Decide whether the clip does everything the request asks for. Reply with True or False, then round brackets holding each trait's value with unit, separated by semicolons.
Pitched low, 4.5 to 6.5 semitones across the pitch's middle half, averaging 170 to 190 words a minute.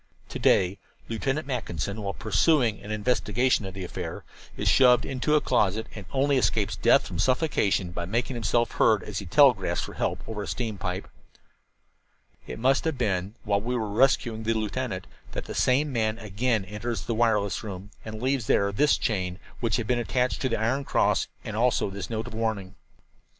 False (110 Hz; 3.8 semitones; 185 wpm)